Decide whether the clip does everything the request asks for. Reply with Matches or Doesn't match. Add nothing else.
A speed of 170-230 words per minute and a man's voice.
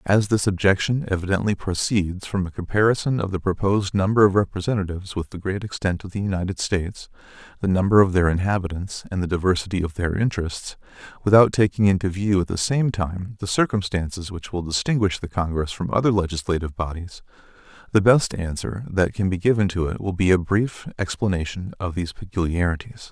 Matches